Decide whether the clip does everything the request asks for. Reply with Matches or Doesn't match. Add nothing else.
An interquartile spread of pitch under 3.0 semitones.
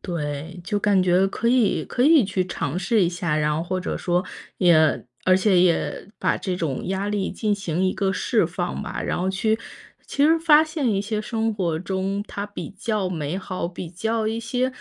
Doesn't match